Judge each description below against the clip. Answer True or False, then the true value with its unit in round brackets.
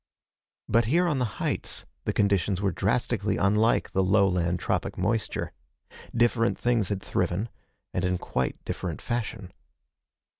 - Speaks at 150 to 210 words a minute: False (135 wpm)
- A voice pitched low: True (100 Hz)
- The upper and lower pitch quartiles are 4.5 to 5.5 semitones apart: False (4.0 semitones)